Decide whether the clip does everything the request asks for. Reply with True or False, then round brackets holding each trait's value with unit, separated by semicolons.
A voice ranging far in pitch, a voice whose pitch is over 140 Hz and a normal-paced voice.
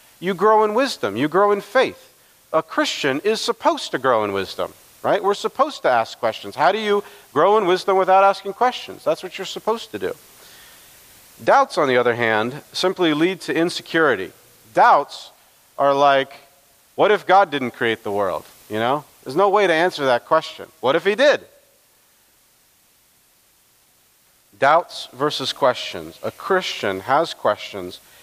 True (7.1 semitones; 185 Hz; 160 wpm)